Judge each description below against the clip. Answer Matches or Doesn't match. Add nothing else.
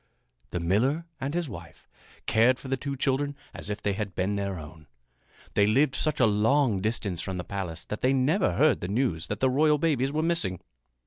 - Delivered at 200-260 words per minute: Matches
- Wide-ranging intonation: Matches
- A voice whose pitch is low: Matches